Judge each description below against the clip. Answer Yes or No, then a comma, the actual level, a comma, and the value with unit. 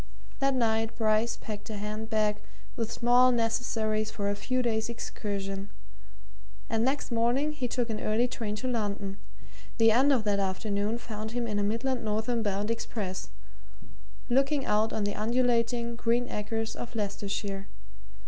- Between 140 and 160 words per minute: Yes, average, 155 wpm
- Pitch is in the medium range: No, high, 225 Hz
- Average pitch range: No, narrow, 2.3 semitones